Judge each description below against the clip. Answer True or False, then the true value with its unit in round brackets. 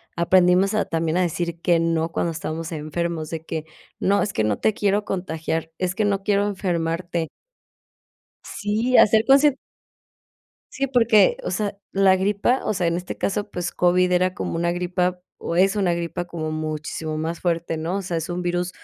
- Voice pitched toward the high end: False (175 Hz)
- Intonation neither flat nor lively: True (3.0 semitones)